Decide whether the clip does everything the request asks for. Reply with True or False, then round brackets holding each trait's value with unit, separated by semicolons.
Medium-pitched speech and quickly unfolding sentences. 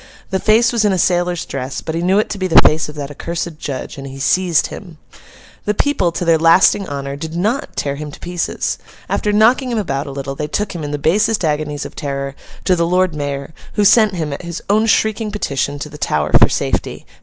True (170 Hz; 235 wpm)